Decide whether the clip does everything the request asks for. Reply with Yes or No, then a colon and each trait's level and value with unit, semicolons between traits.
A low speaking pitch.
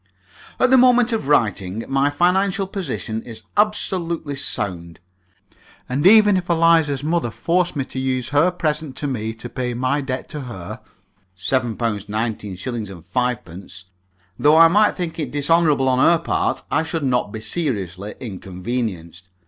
Yes: low, 130 Hz